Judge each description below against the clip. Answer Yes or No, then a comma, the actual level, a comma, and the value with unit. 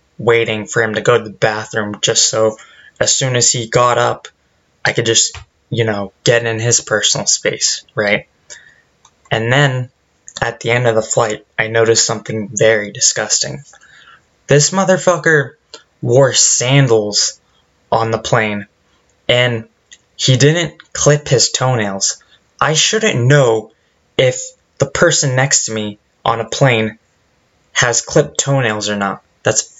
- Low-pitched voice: Yes, low, 115 Hz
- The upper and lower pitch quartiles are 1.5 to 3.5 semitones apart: No, average, 4.2 semitones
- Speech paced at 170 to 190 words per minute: No, average, 145 wpm